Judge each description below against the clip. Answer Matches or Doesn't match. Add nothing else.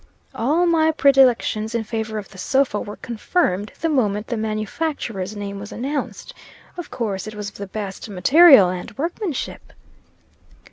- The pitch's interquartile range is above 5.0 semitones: Matches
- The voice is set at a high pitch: Matches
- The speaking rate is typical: Matches